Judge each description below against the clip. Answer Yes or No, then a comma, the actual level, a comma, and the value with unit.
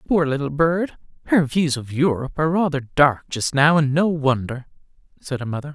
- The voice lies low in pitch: No, medium, 145 Hz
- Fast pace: No, average, 190 wpm